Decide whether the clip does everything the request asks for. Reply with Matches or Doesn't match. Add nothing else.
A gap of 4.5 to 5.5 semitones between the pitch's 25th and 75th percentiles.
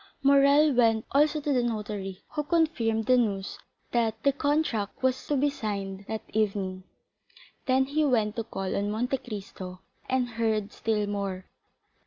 Matches